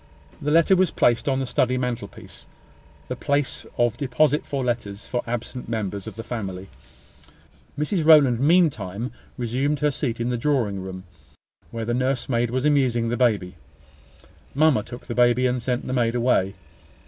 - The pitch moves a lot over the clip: No, average, 3.2 semitones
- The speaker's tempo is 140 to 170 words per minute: Yes, average, 160 wpm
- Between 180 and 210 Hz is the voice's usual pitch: No, low, 125 Hz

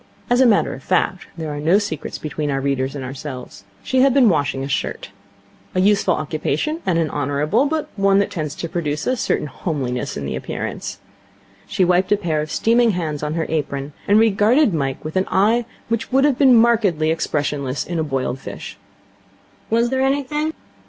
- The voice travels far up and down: Yes, wide, 7.9 semitones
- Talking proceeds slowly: No, average, 195 wpm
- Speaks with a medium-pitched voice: Yes, medium, 170 Hz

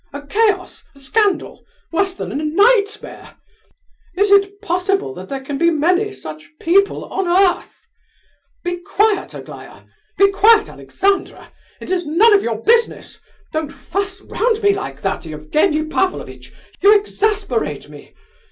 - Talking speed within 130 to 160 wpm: Yes, average, 140 wpm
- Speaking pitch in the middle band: No, very high, 385 Hz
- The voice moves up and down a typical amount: Yes, average, 4.6 semitones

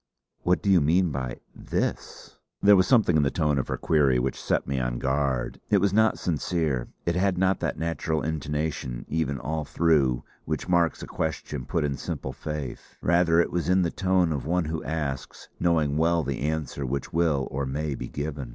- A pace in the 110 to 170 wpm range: No, average, 195 wpm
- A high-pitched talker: No, very low, 80 Hz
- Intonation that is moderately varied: Yes, average, 3.7 semitones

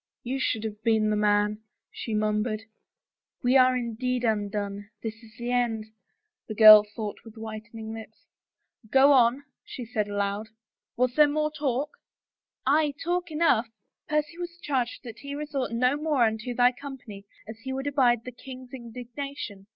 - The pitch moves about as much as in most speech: Yes, average, 3.8 semitones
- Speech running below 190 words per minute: Yes, average, 175 wpm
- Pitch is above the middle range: Yes, high, 240 Hz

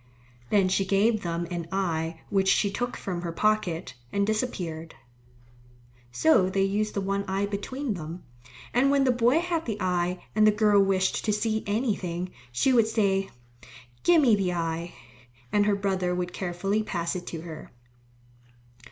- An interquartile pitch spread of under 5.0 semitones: Yes, average, 3.4 semitones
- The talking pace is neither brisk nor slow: Yes, average, 165 wpm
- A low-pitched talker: No, high, 195 Hz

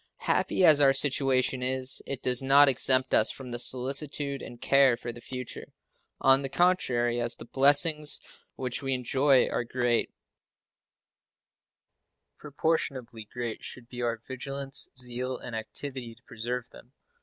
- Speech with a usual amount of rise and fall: No, narrow, 2.2 semitones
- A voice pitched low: Yes, low, 130 Hz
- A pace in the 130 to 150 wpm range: Yes, average, 140 wpm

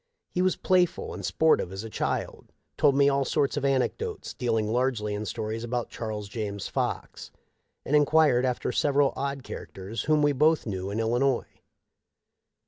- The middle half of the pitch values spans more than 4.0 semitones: Yes, average, 4.8 semitones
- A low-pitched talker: Yes, low, 125 Hz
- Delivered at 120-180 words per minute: Yes, average, 160 wpm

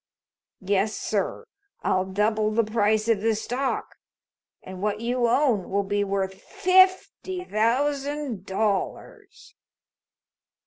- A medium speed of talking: No, slow, 105 wpm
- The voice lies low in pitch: No, high, 220 Hz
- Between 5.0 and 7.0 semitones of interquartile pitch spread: Yes, average, 5.3 semitones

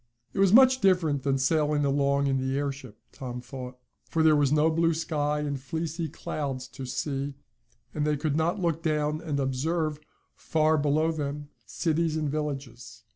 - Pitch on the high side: No, medium, 150 Hz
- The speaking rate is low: No, average, 170 wpm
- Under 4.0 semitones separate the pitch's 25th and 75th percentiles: Yes, narrow, 2.6 semitones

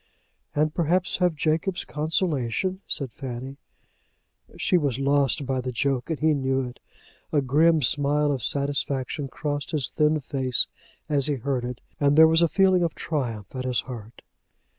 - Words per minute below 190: Yes, average, 160 wpm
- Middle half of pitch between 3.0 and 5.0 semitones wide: Yes, average, 3.3 semitones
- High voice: No, medium, 145 Hz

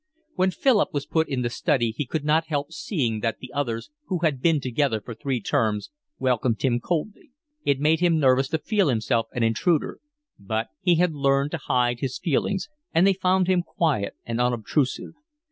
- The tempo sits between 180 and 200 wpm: Yes, average, 190 wpm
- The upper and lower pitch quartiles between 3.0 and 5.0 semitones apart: No, wide, 5.5 semitones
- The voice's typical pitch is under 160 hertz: Yes, medium, 140 Hz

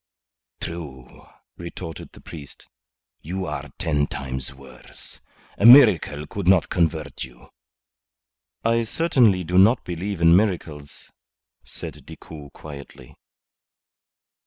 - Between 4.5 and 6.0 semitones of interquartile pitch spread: Yes, average, 5.1 semitones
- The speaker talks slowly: Yes, slow, 105 wpm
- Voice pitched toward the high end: No, very low, 85 Hz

